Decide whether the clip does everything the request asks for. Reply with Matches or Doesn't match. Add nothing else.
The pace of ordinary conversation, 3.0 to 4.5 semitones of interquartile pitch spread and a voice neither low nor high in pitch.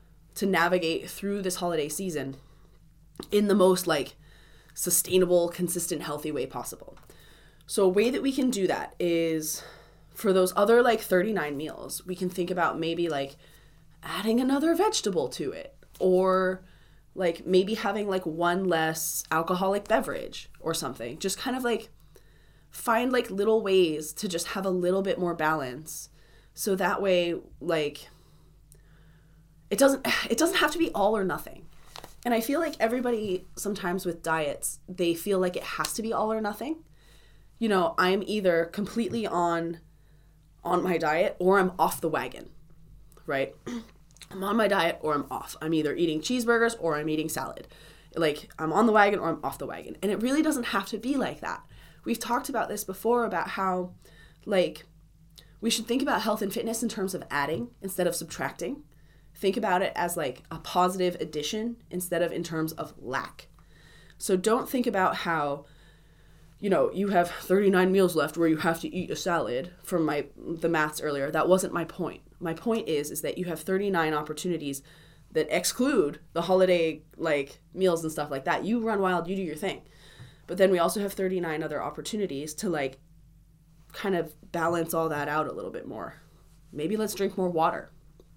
Matches